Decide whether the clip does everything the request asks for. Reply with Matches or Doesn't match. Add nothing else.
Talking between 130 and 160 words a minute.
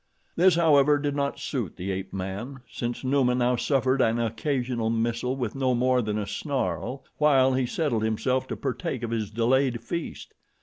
Doesn't match